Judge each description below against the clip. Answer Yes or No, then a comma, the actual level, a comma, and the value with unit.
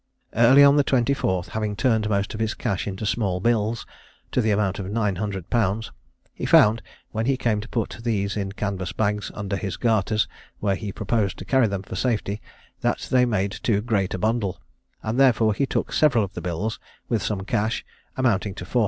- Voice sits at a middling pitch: No, low, 105 Hz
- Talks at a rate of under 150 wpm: No, average, 195 wpm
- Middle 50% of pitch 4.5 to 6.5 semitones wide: No, average, 2.8 semitones